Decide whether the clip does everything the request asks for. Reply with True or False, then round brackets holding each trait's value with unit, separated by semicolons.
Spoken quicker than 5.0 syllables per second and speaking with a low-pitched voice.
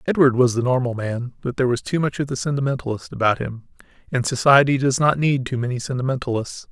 True (6.3 syllables/s; 130 Hz)